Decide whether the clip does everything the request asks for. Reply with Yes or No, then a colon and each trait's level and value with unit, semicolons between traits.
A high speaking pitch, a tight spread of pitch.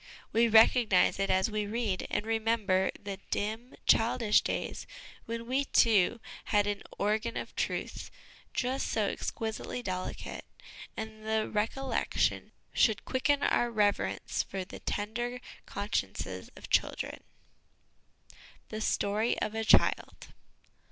Yes: high, 220 Hz; narrow, 2.2 semitones